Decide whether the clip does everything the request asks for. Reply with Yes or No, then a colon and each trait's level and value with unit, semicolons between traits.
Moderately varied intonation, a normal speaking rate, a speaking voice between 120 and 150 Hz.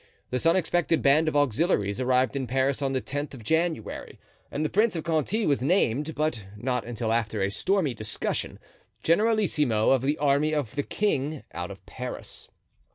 Yes: average, 4.9 semitones; average, 170 wpm; medium, 140 Hz